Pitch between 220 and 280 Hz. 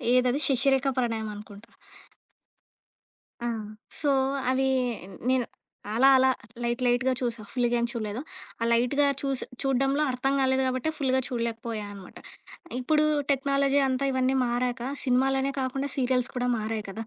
Yes: very high, 255 Hz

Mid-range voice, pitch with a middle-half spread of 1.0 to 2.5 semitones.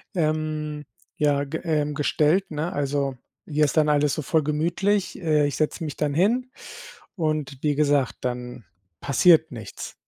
Yes: medium, 150 Hz; narrow, 1.9 semitones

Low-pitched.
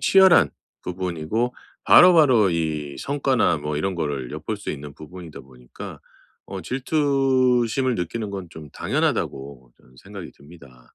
Yes: very low, 90 Hz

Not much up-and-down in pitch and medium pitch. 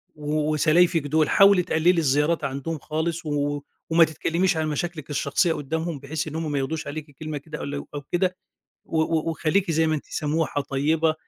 Yes: narrow, 2.0 semitones; medium, 155 Hz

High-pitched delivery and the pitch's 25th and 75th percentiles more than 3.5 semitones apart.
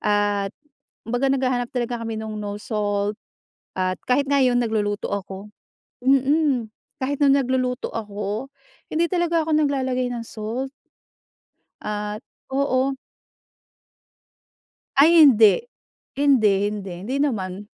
Yes: high, 245 Hz; average, 4.6 semitones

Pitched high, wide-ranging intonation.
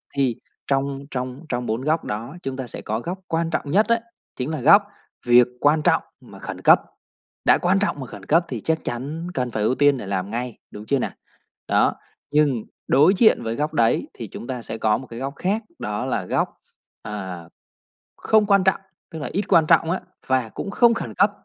No: low, 135 Hz; wide, 5.7 semitones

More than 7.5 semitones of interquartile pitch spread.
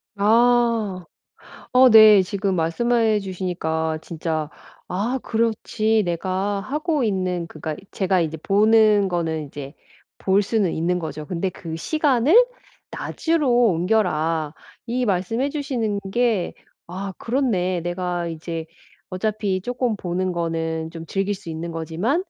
No: average, 5.1 semitones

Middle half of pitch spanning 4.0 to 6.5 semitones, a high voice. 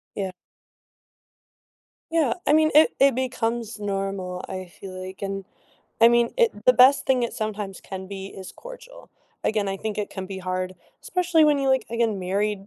Yes: average, 5.1 semitones; high, 215 Hz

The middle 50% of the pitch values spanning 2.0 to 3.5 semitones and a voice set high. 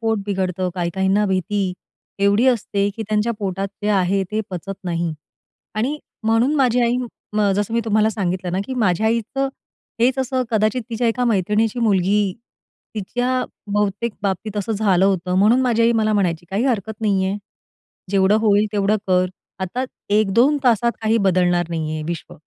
Yes: average, 3.2 semitones; high, 210 Hz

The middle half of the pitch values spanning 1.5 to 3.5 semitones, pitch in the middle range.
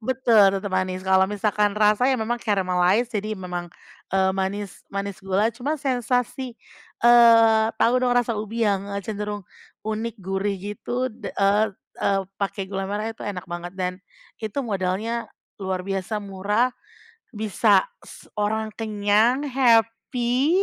No: average, 3.1 semitones; high, 210 Hz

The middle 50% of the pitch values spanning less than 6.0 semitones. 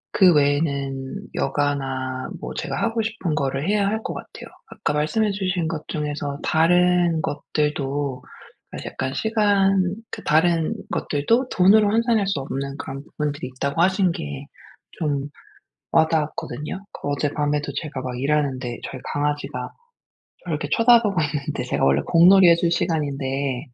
Yes: average, 5.2 semitones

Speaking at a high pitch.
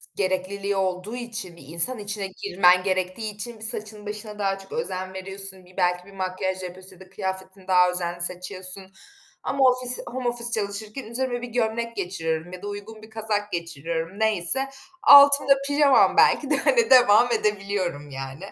Yes: high, 200 Hz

